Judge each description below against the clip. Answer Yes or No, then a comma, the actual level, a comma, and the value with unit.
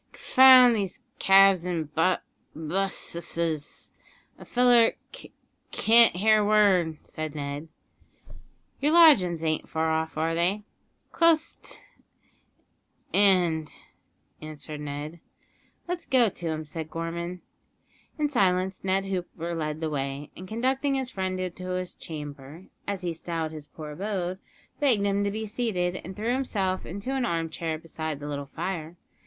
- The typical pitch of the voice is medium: Yes, medium, 180 Hz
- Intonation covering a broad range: No, average, 4.6 semitones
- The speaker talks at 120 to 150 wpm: Yes, average, 140 wpm